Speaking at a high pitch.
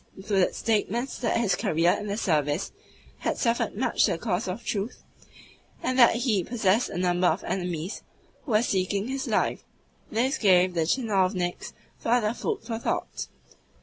Yes: high, 205 Hz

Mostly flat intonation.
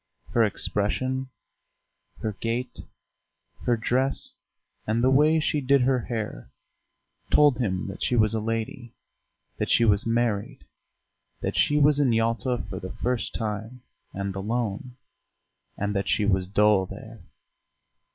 No: average, 3.6 semitones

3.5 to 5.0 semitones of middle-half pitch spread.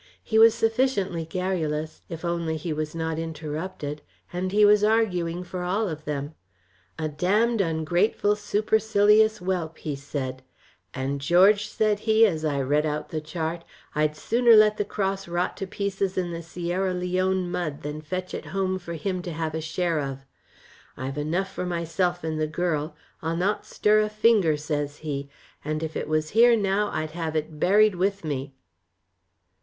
Yes: average, 4.3 semitones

